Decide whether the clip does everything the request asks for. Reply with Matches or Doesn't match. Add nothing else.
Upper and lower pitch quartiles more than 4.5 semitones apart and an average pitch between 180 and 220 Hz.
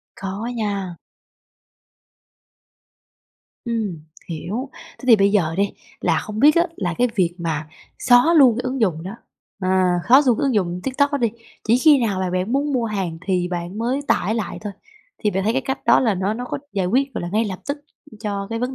Matches